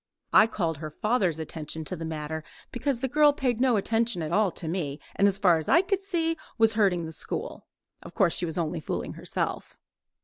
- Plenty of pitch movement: Yes, wide, 7.2 semitones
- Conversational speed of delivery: No, fast, 210 wpm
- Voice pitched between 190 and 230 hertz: Yes, high, 195 Hz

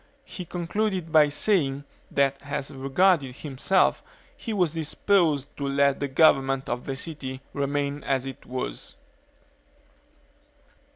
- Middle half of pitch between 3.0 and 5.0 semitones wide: Yes, average, 3.4 semitones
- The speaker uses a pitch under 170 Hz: Yes, medium, 140 Hz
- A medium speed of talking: No, slow, 120 wpm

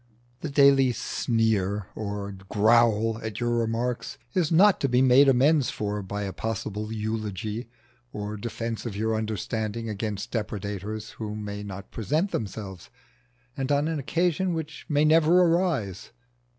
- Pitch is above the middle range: No, low, 115 Hz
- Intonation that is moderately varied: Yes, average, 5.0 semitones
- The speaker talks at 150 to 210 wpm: No, average, 140 wpm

